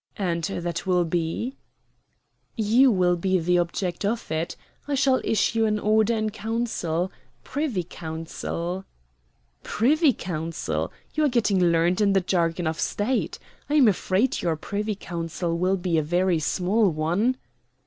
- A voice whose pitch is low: No, medium, 185 Hz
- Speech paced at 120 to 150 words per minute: Yes, average, 145 wpm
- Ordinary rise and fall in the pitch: Yes, average, 4.4 semitones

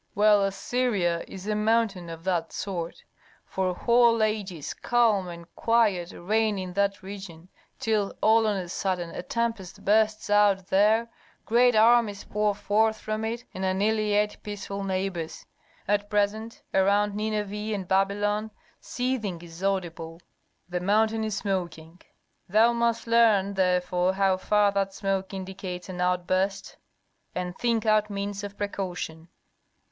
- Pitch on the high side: Yes, high, 200 Hz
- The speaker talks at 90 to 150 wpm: Yes, slow, 135 wpm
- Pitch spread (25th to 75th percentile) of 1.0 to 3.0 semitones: Yes, narrow, 2.6 semitones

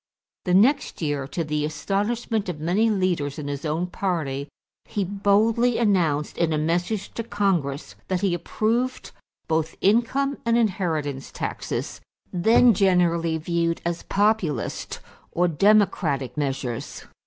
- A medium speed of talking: No, slow, 130 wpm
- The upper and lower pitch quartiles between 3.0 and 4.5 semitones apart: No, average, 5.2 semitones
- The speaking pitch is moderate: Yes, medium, 180 Hz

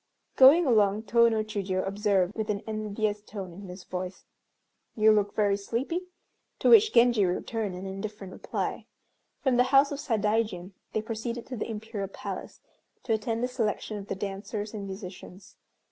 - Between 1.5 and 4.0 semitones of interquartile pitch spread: Yes, average, 2.7 semitones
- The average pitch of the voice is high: Yes, high, 215 Hz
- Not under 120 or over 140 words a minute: No, average, 165 wpm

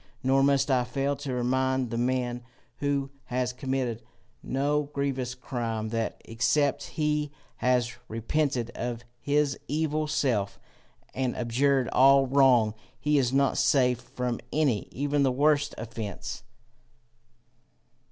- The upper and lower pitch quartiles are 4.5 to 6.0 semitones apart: No, narrow, 2.5 semitones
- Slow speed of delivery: Yes, slow, 125 wpm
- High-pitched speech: No, low, 130 Hz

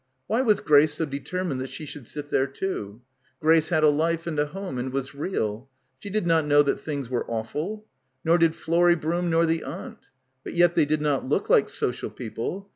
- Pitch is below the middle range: No, medium, 155 Hz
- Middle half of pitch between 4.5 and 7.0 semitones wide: No, average, 3.8 semitones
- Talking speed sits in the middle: No, fast, 215 wpm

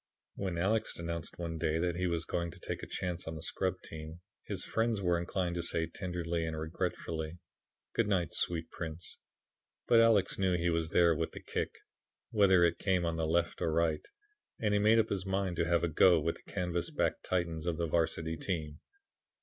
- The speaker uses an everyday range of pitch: No, narrow, 2.1 semitones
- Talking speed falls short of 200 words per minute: No, fast, 205 wpm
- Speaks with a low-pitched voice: Yes, very low, 85 Hz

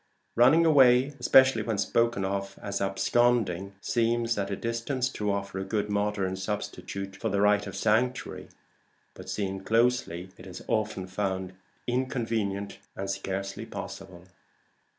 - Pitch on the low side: Yes, low, 105 Hz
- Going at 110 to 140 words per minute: Yes, slow, 135 wpm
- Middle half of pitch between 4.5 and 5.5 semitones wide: No, average, 3.4 semitones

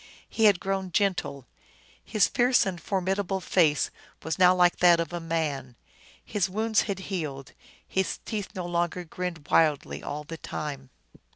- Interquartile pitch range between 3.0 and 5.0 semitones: Yes, average, 3.3 semitones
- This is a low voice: No, medium, 180 Hz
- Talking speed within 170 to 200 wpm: No, average, 155 wpm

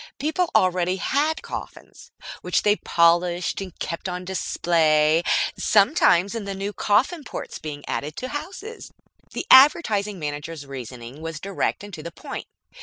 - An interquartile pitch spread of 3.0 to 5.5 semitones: Yes, average, 5.1 semitones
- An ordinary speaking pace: Yes, average, 145 wpm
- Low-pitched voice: No, medium, 185 Hz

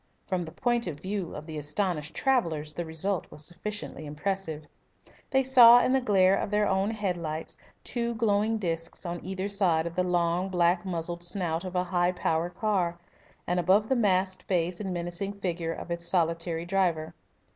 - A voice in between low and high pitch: Yes, medium, 180 Hz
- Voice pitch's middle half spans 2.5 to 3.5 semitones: Yes, average, 3.1 semitones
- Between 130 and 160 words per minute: No, average, 180 wpm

